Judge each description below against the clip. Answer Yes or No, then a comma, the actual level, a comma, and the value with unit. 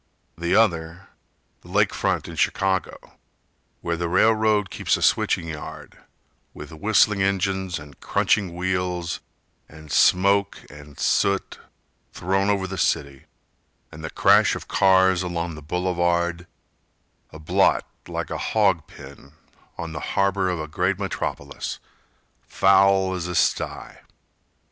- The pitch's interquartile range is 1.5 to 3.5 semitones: Yes, average, 2.7 semitones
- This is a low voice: Yes, very low, 90 Hz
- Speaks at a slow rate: Yes, slow, 130 wpm